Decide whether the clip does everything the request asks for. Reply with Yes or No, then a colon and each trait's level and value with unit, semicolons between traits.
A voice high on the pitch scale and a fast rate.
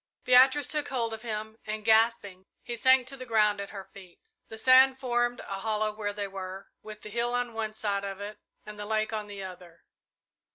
Yes: high, 215 Hz; fast, 210 wpm